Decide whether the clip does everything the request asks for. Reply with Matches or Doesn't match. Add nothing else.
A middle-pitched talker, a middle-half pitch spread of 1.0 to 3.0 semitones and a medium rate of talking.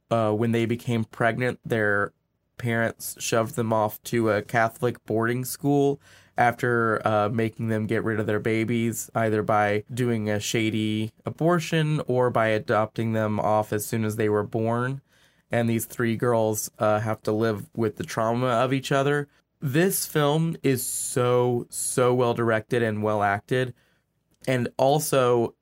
Doesn't match